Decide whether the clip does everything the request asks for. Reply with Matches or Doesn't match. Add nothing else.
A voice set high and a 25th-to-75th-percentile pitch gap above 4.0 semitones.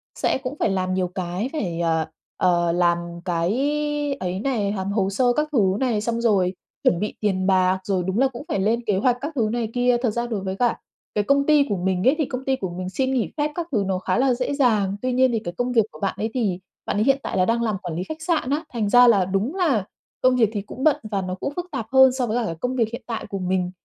Matches